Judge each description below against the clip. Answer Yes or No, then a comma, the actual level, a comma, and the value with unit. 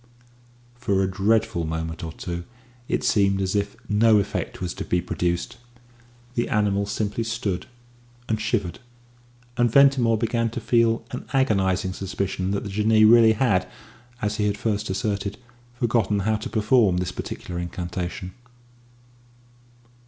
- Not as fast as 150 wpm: Yes, average, 140 wpm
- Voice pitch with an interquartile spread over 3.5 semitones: No, average, 3.2 semitones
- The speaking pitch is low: Yes, low, 105 Hz